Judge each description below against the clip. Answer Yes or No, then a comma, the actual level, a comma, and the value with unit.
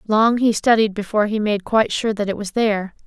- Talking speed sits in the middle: No, fast, 235 wpm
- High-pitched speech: Yes, high, 210 Hz